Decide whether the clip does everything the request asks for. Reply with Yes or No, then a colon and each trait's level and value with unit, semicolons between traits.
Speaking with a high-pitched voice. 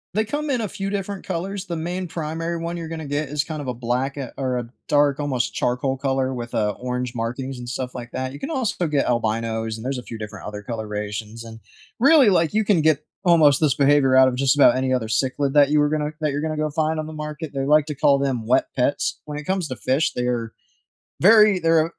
No: medium, 140 Hz